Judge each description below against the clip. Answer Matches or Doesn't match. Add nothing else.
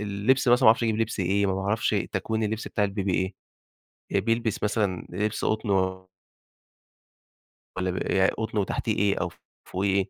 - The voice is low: Matches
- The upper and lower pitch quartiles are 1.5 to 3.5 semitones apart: Matches